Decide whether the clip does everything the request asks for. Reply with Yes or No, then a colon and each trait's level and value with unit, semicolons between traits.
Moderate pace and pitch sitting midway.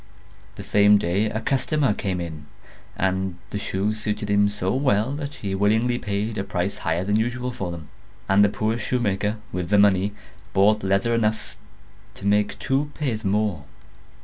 No: average, 170 wpm; low, 105 Hz